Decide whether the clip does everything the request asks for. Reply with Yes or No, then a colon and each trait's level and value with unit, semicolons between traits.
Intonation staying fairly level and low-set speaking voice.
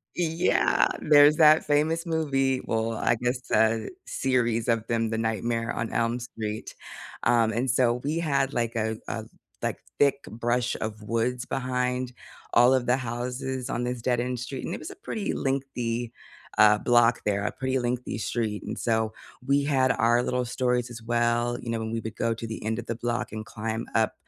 Yes: narrow, 2.3 semitones; low, 120 Hz